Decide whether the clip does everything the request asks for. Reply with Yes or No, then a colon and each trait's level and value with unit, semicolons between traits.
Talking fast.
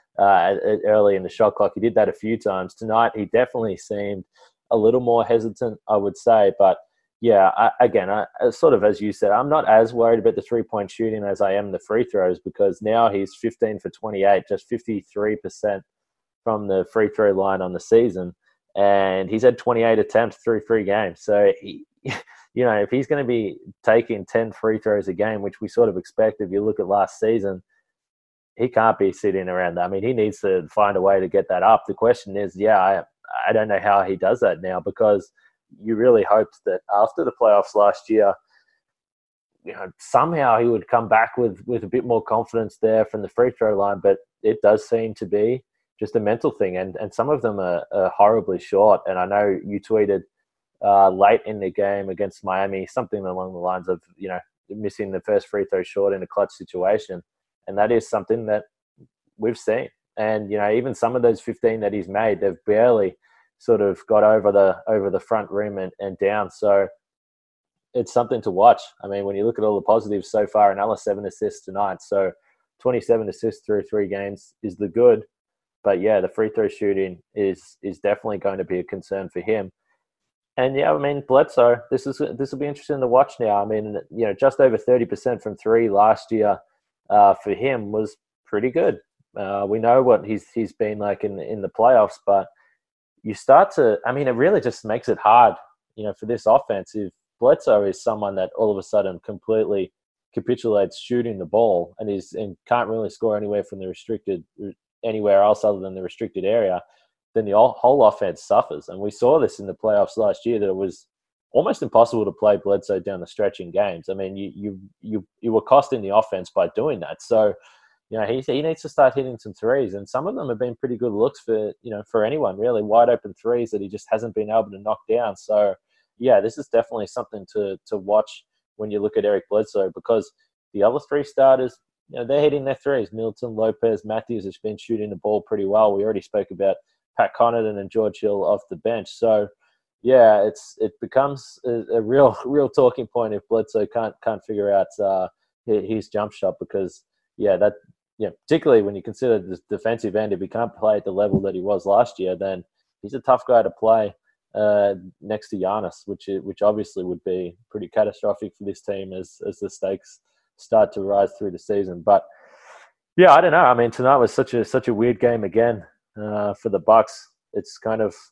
Yes: fast, 215 wpm